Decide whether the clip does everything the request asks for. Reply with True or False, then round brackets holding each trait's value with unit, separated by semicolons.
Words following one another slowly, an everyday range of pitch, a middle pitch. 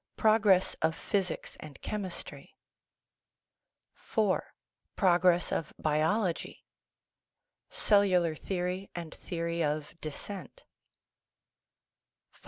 True (75 wpm; 3.6 semitones; 180 Hz)